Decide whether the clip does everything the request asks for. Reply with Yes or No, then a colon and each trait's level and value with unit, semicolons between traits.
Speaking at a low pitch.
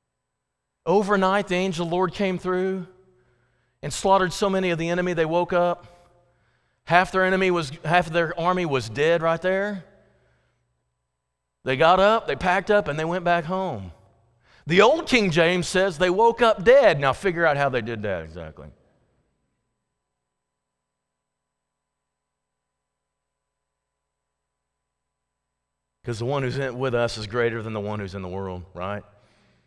No: medium, 150 Hz